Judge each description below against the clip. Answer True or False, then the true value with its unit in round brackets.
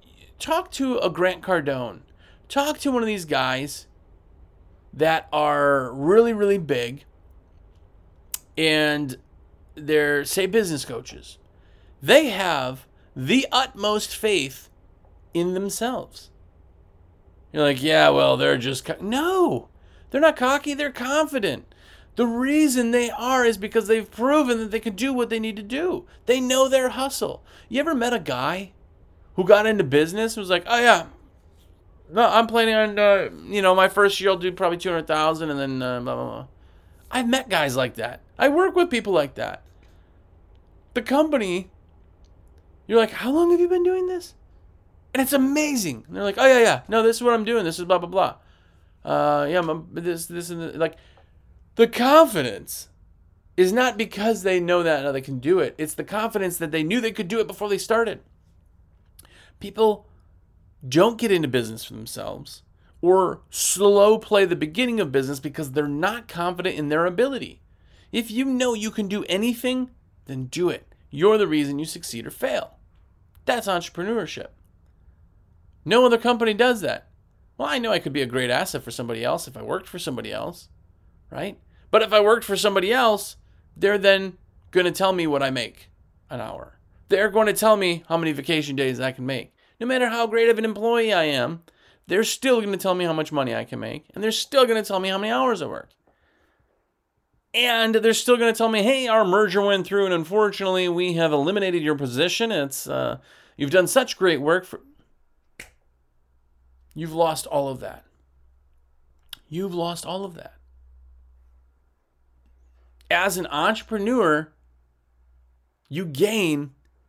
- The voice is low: False (175 Hz)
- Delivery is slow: False (175 wpm)